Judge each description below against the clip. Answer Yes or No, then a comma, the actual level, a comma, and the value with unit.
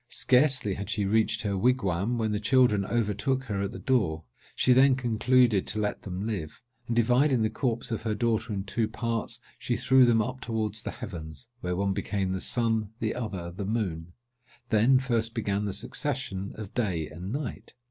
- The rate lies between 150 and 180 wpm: No, average, 190 wpm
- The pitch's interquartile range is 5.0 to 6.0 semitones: No, average, 3.6 semitones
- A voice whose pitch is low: Yes, low, 110 Hz